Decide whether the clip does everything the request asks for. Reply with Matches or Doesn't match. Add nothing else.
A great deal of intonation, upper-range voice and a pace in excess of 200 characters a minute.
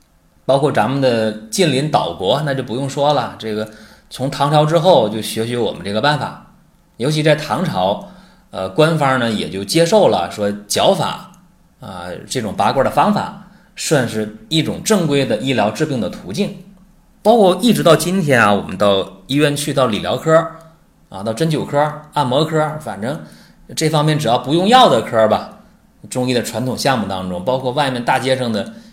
Doesn't match